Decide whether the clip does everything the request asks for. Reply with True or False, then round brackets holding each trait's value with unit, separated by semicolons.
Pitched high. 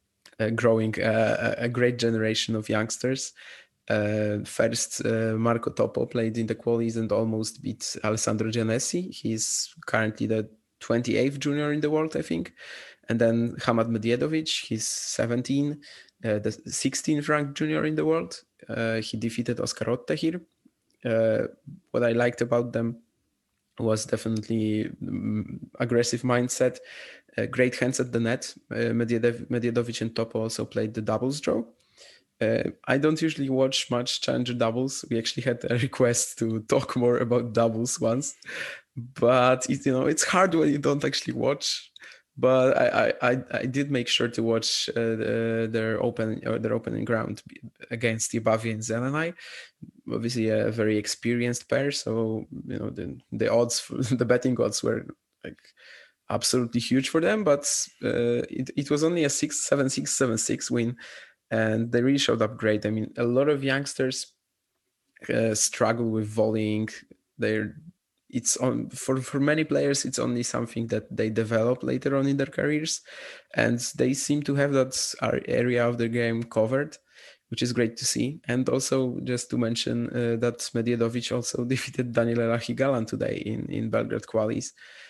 False (120 Hz)